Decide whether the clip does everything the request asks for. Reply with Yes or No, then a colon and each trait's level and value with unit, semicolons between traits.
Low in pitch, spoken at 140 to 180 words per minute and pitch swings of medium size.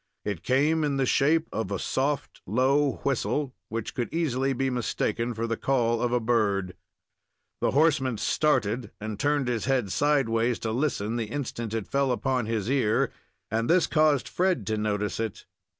Yes: low, 125 Hz; average, 170 wpm; average, 3.9 semitones